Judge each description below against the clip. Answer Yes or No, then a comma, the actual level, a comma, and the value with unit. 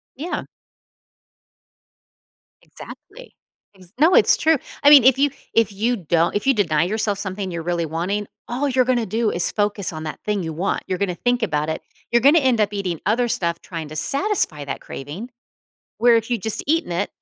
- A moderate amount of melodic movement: No, wide, 6.2 semitones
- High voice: Yes, high, 205 Hz